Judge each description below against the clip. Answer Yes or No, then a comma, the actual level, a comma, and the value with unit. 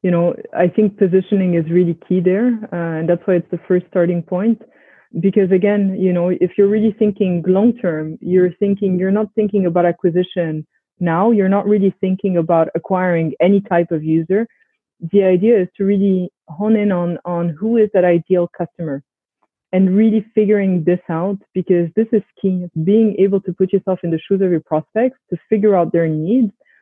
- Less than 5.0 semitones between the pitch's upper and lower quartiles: Yes, average, 2.8 semitones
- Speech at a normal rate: Yes, average, 190 wpm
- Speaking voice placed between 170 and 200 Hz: Yes, medium, 185 Hz